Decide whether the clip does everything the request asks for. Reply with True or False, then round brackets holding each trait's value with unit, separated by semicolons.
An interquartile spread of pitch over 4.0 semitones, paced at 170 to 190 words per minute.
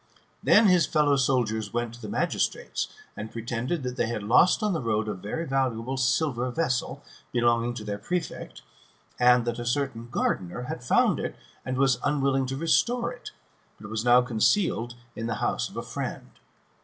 False (3.3 semitones; 180 wpm)